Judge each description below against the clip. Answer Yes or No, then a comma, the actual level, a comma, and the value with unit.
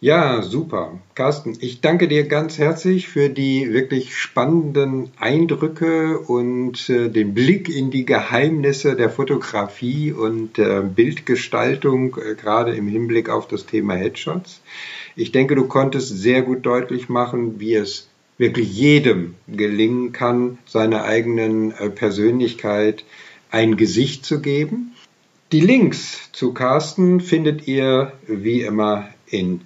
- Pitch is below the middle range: Yes, low, 125 Hz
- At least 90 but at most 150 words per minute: Yes, average, 130 wpm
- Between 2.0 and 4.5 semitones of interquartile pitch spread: No, average, 4.9 semitones